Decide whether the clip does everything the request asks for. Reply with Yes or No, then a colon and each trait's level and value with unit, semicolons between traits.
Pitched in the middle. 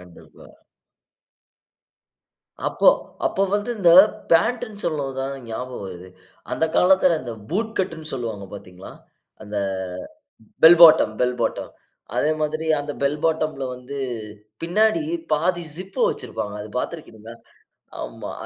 Yes: medium, 155 Hz